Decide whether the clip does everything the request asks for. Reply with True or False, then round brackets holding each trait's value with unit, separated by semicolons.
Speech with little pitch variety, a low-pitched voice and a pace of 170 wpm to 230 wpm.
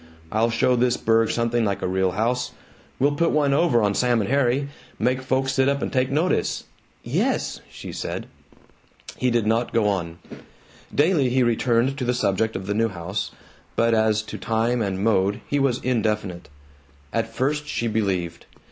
False (3.5 semitones; 115 Hz; 175 wpm)